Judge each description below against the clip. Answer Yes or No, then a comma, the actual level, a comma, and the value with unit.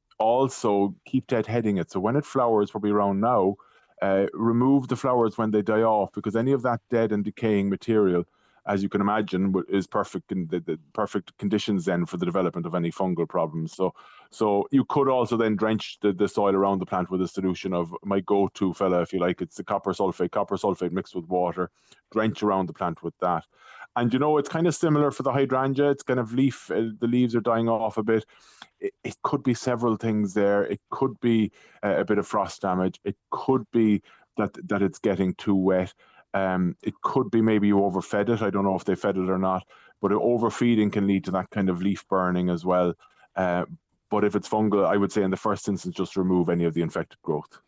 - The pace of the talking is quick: Yes, fast, 225 wpm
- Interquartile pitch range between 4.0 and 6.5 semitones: No, average, 3.6 semitones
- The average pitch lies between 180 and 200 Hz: No, low, 105 Hz